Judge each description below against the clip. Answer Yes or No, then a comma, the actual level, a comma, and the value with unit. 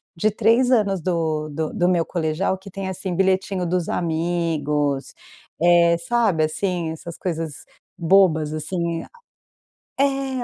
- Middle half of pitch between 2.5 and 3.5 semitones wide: Yes, average, 3.2 semitones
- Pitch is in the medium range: Yes, medium, 175 Hz